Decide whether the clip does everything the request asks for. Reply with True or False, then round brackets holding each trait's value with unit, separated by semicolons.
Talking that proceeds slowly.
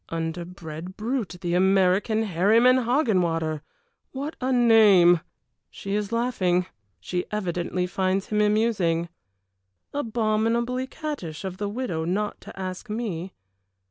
True (110 wpm)